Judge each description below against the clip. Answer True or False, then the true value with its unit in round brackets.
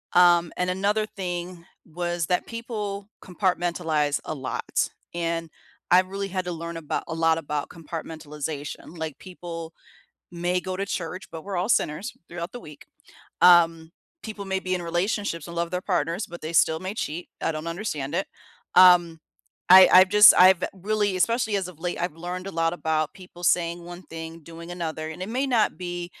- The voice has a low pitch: False (175 Hz)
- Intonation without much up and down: True (2.2 semitones)